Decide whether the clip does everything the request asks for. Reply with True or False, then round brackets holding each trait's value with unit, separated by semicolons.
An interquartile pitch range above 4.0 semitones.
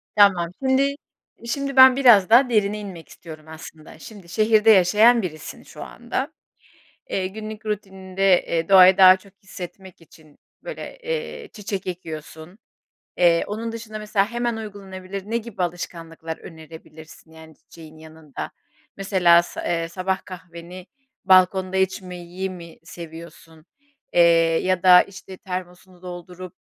False (3.5 semitones)